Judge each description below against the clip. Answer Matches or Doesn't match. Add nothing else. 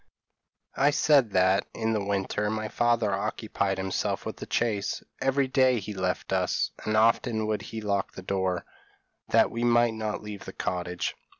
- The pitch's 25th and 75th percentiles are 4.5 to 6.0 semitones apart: Doesn't match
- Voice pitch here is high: Doesn't match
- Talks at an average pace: Matches